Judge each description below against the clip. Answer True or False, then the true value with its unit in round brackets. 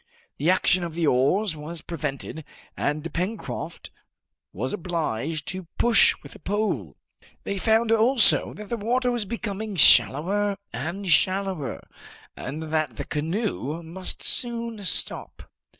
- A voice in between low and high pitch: True (180 Hz)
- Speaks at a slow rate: True (130 wpm)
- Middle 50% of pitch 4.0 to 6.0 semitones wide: True (5.6 semitones)